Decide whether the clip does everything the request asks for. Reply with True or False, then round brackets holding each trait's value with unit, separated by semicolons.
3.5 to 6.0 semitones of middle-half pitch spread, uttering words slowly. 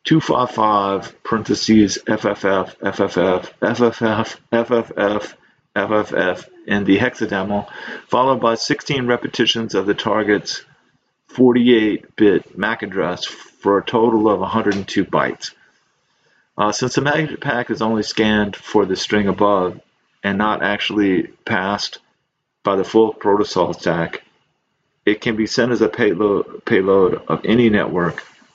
False (2.8 semitones; 125 wpm)